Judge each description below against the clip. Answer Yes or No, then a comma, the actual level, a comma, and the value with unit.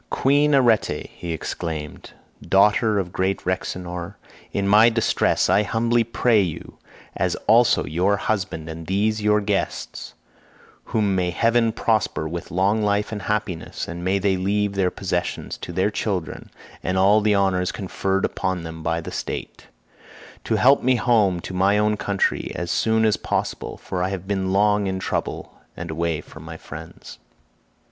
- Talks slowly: No, average, 160 wpm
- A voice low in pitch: Yes, low, 100 Hz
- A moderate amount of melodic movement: Yes, average, 3.0 semitones